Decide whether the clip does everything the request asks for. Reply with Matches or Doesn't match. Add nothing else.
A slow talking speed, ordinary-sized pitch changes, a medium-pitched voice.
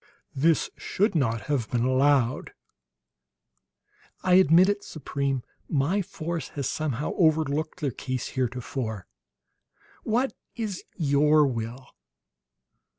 Matches